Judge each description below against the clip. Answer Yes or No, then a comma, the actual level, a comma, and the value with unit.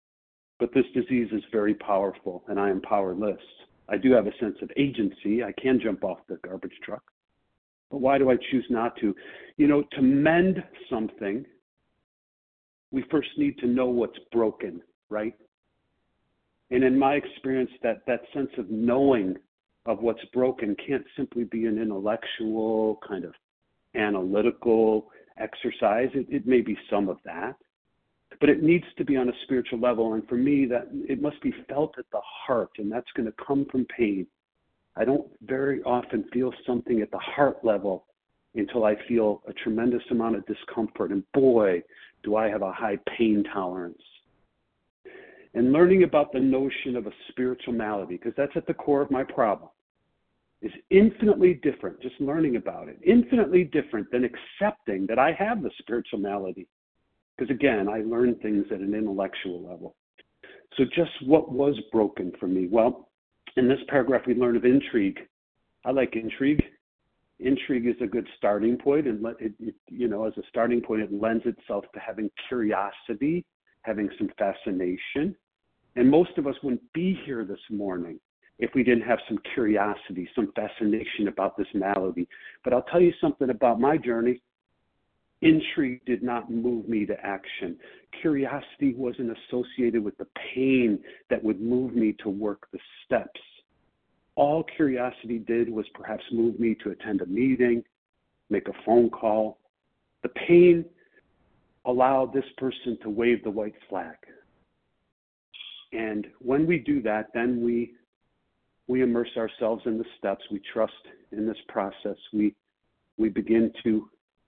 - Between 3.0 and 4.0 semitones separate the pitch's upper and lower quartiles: Yes, average, 3.6 semitones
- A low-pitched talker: Yes, low, 120 Hz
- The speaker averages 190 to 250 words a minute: No, average, 160 wpm